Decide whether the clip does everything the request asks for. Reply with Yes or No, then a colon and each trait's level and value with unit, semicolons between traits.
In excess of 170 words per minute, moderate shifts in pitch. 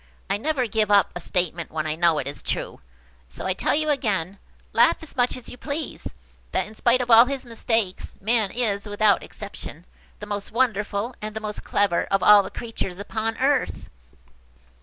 Yes: average, 185 wpm; average, 3.8 semitones